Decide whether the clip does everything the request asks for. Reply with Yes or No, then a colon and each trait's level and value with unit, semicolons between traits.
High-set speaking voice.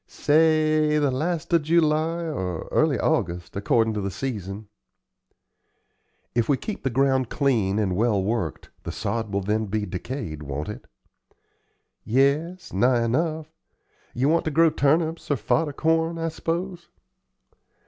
No: low, 135 Hz